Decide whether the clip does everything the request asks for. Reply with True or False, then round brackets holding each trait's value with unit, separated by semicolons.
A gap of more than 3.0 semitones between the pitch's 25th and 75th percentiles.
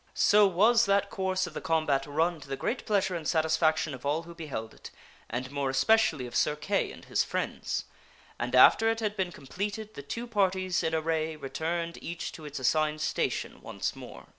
True (4.7 semitones)